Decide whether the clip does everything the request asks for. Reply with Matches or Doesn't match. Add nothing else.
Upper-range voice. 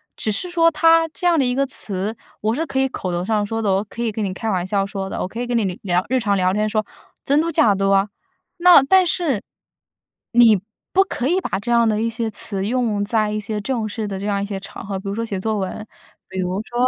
Matches